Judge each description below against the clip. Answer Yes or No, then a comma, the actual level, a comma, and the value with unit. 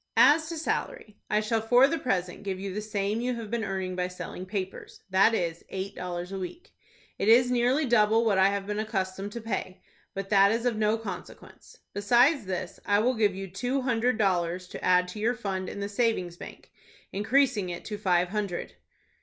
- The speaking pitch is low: No, high, 205 Hz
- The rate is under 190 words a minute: No, average, 200 wpm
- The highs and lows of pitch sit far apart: No, average, 3.8 semitones